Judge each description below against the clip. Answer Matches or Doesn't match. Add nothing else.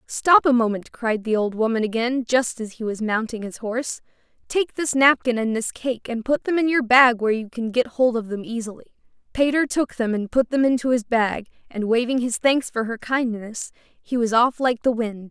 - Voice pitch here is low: Doesn't match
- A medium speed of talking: Doesn't match